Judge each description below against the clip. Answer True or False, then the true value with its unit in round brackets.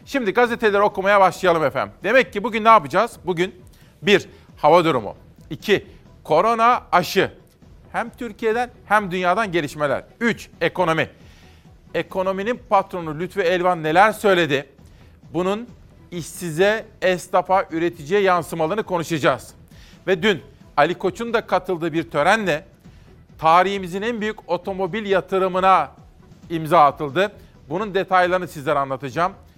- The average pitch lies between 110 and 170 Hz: False (185 Hz)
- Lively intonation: False (3.6 semitones)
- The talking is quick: False (110 wpm)